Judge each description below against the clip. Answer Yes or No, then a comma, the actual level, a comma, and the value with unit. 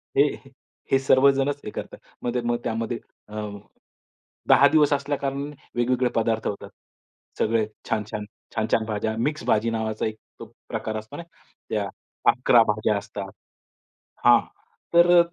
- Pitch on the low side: Yes, low, 115 Hz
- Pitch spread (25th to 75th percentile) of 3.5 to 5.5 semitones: Yes, average, 4.0 semitones